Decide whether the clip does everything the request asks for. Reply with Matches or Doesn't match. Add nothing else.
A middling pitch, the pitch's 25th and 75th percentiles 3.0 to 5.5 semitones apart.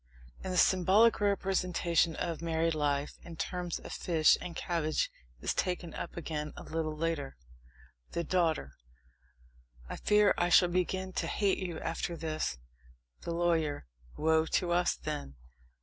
Doesn't match